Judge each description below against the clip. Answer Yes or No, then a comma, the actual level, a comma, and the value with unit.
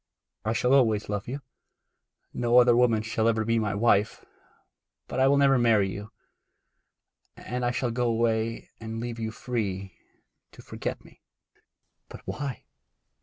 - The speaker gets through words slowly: No, average, 150 wpm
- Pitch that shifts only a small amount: Yes, narrow, 2.0 semitones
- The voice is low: Yes, low, 115 Hz